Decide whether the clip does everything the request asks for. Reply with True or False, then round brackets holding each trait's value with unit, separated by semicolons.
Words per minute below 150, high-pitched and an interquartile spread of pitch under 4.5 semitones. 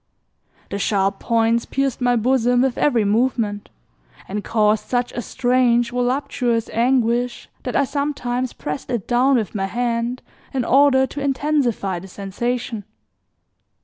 True (135 wpm; 240 Hz; 2.6 semitones)